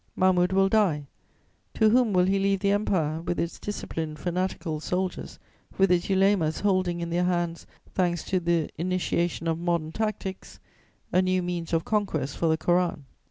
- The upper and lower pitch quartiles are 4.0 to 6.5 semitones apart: No, narrow, 2.4 semitones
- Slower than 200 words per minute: Yes, average, 165 wpm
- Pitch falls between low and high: Yes, medium, 180 Hz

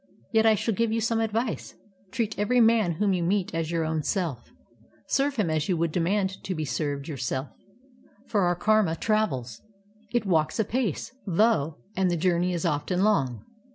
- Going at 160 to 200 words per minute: Yes, average, 180 wpm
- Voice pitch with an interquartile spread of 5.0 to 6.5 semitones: Yes, average, 5.3 semitones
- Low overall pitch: No, medium, 185 Hz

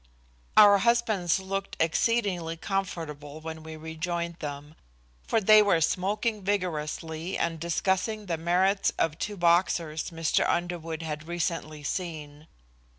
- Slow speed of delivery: Yes, slow, 120 wpm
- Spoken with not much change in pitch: No, average, 3.4 semitones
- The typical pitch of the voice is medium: Yes, medium, 170 Hz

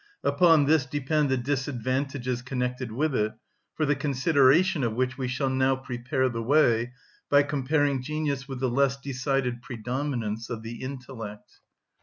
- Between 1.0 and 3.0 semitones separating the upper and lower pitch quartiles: Yes, narrow, 2.4 semitones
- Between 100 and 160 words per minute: Yes, average, 150 wpm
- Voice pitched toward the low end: Yes, low, 130 Hz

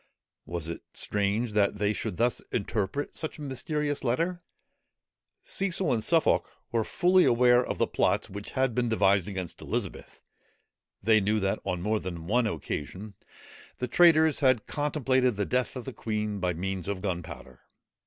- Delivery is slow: No, average, 160 wpm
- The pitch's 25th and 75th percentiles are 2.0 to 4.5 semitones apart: No, average, 5.1 semitones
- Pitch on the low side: Yes, low, 110 Hz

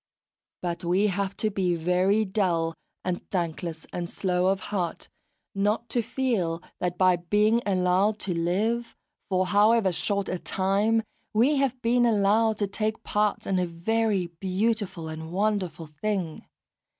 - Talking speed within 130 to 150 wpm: Yes, average, 145 wpm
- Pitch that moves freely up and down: No, average, 3.3 semitones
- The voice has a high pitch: Yes, high, 195 Hz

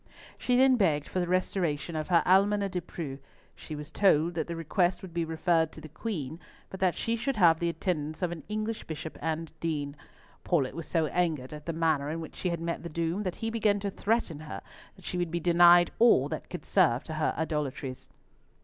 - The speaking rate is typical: No, fast, 220 wpm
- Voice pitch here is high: No, medium, 170 Hz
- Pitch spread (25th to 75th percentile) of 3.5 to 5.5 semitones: No, average, 3.0 semitones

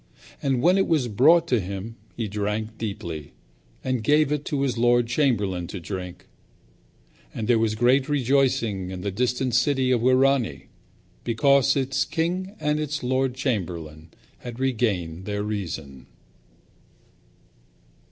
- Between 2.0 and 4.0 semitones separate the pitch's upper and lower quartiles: No, average, 5.1 semitones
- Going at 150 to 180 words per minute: No, slow, 135 wpm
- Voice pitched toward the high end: No, low, 120 Hz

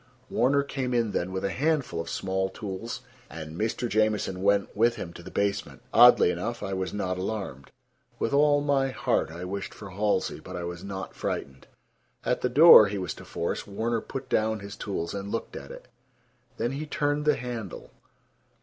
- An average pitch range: Yes, average, 4.9 semitones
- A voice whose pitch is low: Yes, low, 105 Hz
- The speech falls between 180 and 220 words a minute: Yes, average, 190 wpm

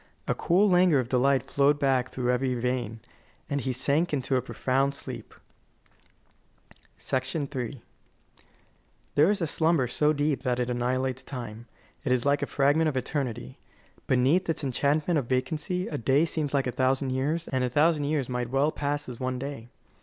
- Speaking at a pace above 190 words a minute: No, average, 170 wpm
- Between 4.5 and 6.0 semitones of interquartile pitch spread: No, average, 2.8 semitones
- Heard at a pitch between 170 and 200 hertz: No, low, 135 Hz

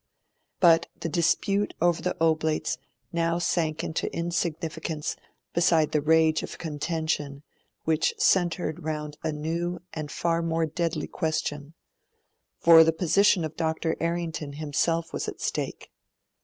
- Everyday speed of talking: No, slow, 130 wpm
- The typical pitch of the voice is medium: Yes, medium, 160 Hz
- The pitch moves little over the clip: Yes, narrow, 1.5 semitones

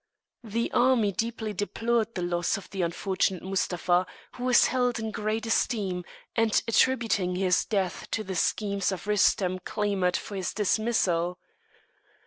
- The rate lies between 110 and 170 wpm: Yes, average, 140 wpm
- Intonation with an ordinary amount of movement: Yes, average, 3.7 semitones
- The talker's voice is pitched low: No, high, 205 Hz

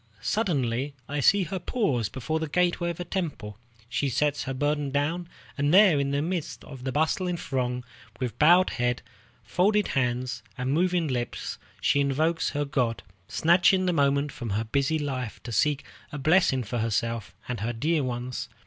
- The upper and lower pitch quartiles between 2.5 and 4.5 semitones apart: No, average, 5.1 semitones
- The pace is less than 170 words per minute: No, average, 175 wpm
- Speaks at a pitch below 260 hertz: Yes, medium, 140 Hz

